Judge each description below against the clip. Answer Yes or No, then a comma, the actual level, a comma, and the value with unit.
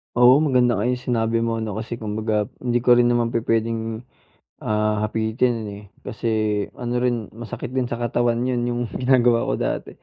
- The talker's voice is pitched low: Yes, low, 115 Hz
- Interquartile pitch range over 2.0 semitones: No, narrow, 1.7 semitones